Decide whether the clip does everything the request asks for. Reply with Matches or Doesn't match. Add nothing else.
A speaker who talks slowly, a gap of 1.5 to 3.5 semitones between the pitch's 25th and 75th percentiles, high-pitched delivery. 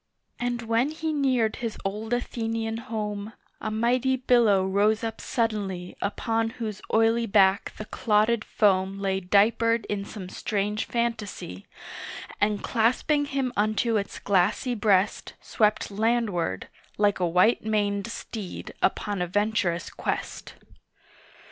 Matches